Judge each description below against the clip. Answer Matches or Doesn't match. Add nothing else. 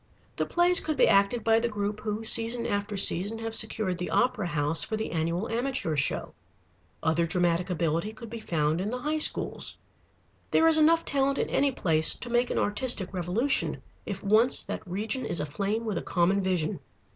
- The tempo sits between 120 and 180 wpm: Doesn't match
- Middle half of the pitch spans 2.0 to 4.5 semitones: Doesn't match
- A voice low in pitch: Doesn't match